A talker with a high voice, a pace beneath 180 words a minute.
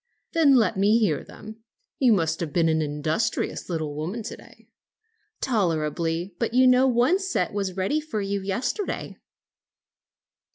Yes: high, 200 Hz; average, 150 wpm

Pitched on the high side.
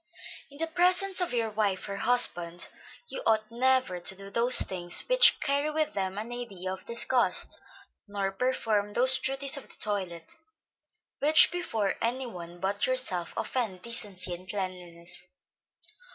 Yes: high, 215 Hz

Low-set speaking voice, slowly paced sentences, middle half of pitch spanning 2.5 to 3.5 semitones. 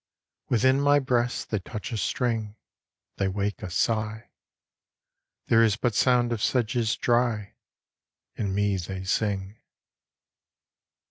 Yes: low, 110 Hz; slow, 120 wpm; average, 2.9 semitones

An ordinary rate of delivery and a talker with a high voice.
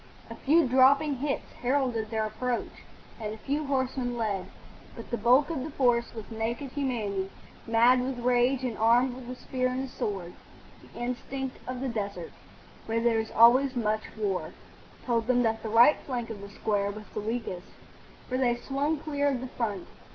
Yes: average, 185 wpm; high, 245 Hz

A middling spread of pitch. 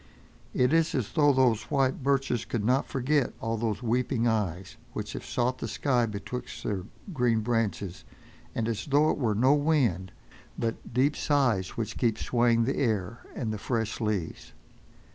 Yes: average, 3.3 semitones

